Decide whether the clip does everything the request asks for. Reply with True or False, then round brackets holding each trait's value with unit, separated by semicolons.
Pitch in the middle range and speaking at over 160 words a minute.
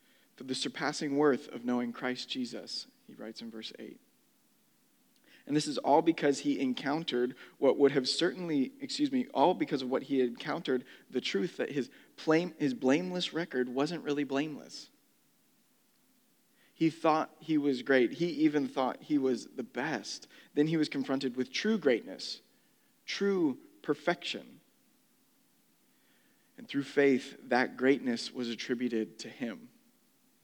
False (160 Hz; 145 wpm)